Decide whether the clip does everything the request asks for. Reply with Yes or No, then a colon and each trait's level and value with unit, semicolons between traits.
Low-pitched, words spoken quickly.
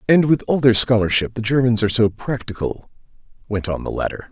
No: low, 115 Hz; average, 195 wpm